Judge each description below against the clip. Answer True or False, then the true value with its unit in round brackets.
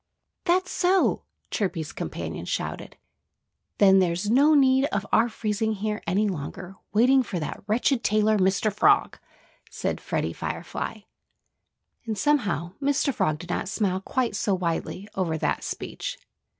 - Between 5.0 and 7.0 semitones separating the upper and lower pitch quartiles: True (5.6 semitones)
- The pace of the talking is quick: False (135 wpm)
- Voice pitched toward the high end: True (210 Hz)